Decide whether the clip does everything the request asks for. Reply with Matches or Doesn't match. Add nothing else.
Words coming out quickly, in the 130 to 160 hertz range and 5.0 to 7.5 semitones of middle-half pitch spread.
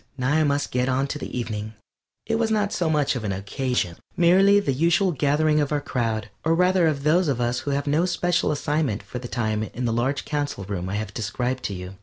Matches